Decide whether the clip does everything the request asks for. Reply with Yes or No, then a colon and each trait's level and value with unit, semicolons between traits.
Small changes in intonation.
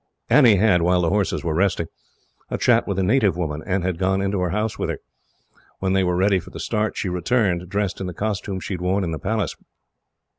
Yes: narrow, 2.3 semitones